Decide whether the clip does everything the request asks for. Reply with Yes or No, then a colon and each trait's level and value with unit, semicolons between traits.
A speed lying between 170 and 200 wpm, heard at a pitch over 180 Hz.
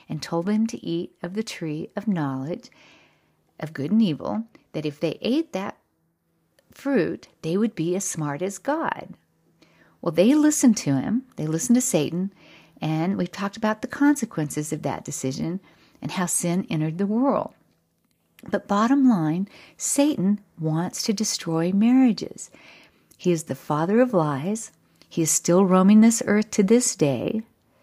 No: average, 160 wpm; high, 190 Hz